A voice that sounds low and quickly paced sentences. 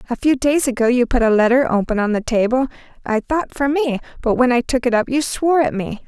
No: very high, 250 Hz; fast, 255 wpm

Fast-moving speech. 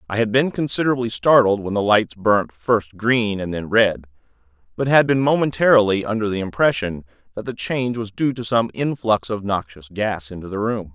No: average, 190 wpm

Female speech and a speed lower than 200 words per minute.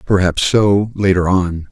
No: male; average, 140 wpm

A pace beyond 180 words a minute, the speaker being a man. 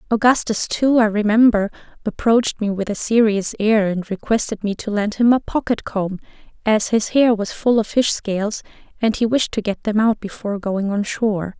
No: average, 195 wpm; female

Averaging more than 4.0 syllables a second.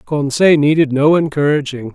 Yes: 5.0 syllables/s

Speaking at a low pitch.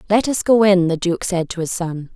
No: medium, 185 Hz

